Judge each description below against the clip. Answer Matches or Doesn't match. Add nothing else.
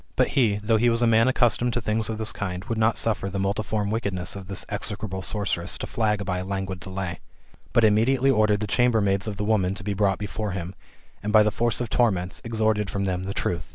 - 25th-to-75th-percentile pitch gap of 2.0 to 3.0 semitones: Matches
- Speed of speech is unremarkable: Doesn't match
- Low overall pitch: Matches